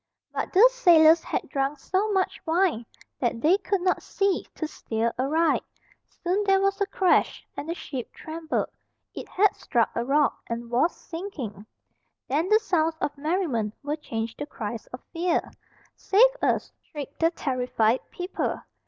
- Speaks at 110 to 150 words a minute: No, average, 160 wpm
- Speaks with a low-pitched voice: No, very high, 315 Hz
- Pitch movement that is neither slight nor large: No, wide, 6.8 semitones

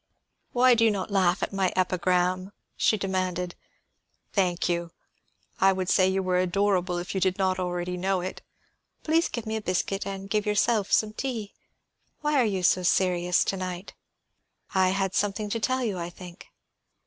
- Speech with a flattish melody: Yes, narrow, 2.3 semitones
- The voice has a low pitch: No, high, 190 Hz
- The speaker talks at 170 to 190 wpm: Yes, average, 175 wpm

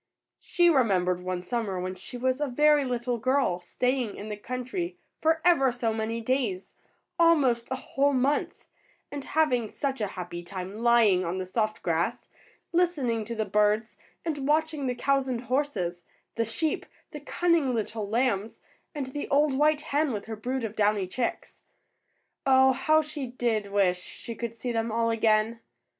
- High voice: Yes, high, 240 Hz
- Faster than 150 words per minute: Yes, average, 170 wpm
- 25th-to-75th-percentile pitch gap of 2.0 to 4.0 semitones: No, average, 4.7 semitones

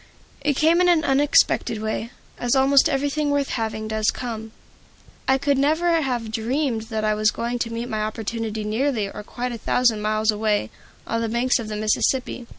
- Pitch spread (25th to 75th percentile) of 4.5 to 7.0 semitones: No, average, 3.8 semitones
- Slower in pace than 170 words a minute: No, average, 185 wpm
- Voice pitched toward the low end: No, high, 235 Hz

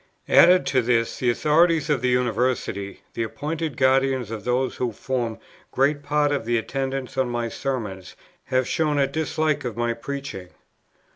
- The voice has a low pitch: Yes, low, 130 Hz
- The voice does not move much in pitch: No, average, 3.4 semitones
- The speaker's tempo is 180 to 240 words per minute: No, average, 160 wpm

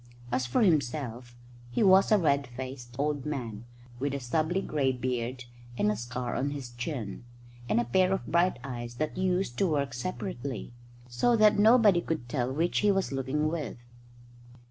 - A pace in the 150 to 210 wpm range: Yes, average, 170 wpm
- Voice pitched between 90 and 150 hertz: Yes, medium, 140 Hz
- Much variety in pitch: Yes, wide, 6.0 semitones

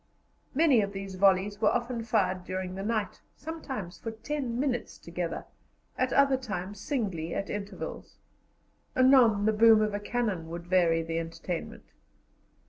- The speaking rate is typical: Yes, average, 145 wpm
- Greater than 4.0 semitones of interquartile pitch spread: Yes, average, 4.8 semitones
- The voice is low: No, high, 205 Hz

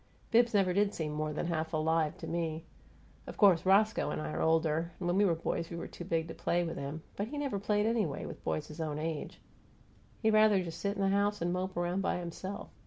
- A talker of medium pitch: Yes, medium, 175 Hz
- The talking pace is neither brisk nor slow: No, fast, 240 wpm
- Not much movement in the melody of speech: No, average, 3.9 semitones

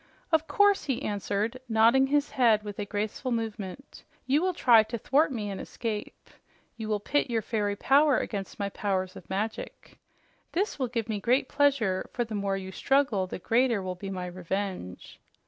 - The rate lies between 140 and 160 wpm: No, average, 180 wpm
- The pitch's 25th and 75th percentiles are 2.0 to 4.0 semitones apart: No, average, 4.8 semitones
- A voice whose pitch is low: No, high, 220 Hz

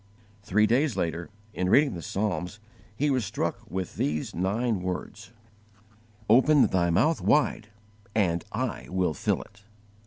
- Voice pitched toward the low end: Yes, low, 100 Hz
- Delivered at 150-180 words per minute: No, slow, 135 wpm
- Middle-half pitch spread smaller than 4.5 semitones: No, average, 5.2 semitones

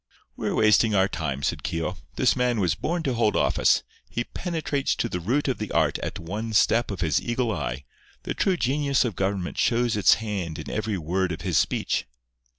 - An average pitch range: No, wide, 5.9 semitones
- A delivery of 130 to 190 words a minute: No, average, 200 wpm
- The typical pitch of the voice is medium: No, low, 105 Hz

